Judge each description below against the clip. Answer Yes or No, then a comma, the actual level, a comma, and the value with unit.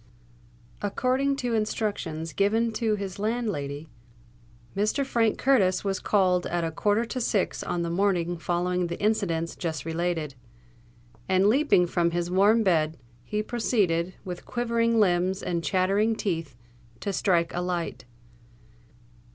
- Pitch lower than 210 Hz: Yes, high, 190 Hz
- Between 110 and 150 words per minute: Yes, slow, 135 wpm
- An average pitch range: Yes, average, 4.2 semitones